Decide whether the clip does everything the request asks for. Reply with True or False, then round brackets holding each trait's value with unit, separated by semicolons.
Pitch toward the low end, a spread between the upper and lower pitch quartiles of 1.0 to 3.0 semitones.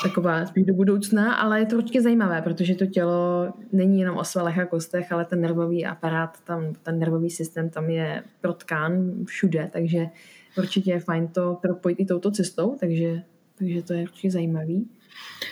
False (180 Hz; 2.4 semitones)